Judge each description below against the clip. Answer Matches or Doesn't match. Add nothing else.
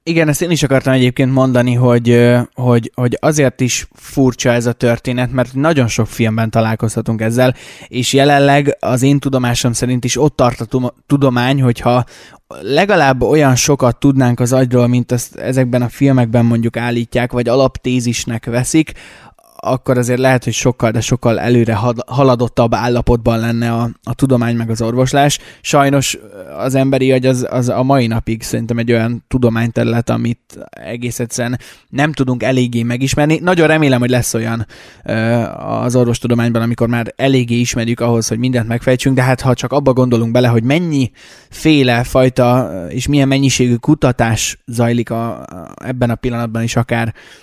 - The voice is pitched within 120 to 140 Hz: Matches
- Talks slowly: Doesn't match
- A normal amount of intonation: Doesn't match